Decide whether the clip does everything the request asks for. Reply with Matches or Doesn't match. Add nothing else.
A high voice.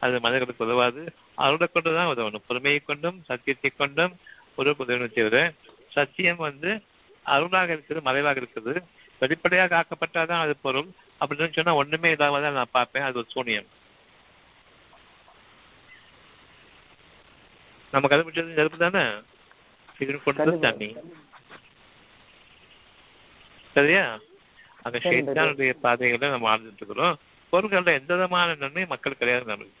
Doesn't match